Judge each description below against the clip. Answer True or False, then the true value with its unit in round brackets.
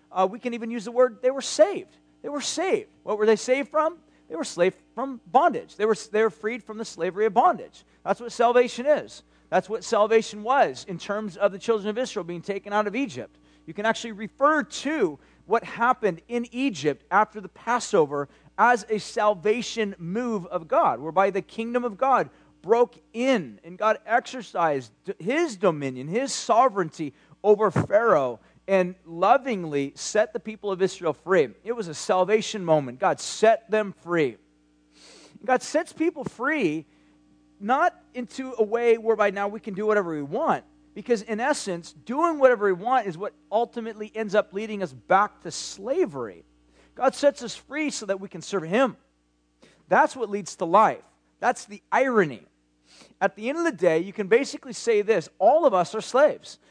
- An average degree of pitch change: True (5.0 semitones)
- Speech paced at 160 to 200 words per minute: True (180 wpm)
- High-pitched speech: True (215 Hz)